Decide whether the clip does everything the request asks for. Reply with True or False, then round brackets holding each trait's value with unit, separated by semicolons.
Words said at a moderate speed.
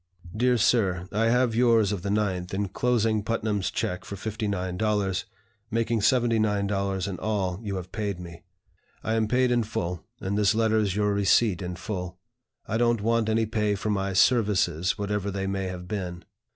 True (170 wpm)